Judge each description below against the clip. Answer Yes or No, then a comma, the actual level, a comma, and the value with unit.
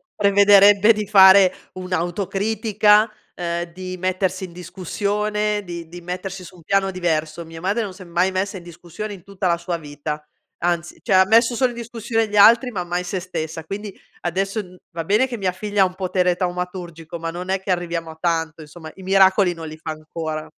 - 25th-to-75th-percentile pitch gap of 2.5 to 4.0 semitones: Yes, average, 2.9 semitones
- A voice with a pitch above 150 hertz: Yes, medium, 185 Hz